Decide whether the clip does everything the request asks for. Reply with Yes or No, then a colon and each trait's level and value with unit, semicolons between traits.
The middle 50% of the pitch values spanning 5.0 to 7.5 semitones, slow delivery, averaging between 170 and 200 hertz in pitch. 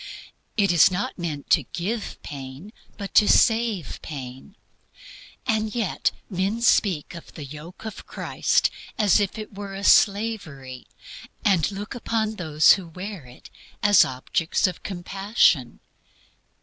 Yes: average, 5.3 semitones; slow, 130 wpm; high, 190 Hz